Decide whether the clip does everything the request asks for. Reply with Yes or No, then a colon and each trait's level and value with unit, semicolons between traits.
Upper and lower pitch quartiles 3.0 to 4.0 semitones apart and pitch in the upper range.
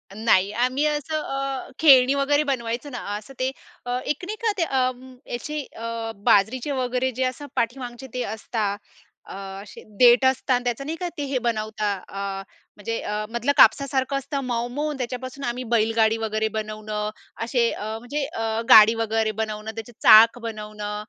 Yes: average, 3.4 semitones; high, 240 Hz